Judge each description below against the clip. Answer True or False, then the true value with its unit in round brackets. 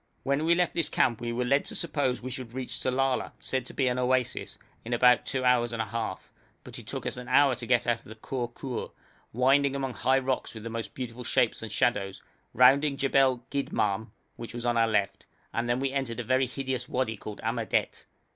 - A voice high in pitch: False (125 Hz)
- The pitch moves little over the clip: True (2.3 semitones)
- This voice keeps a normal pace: False (220 wpm)